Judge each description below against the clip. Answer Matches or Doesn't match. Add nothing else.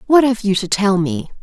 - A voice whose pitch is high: Matches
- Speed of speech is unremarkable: Doesn't match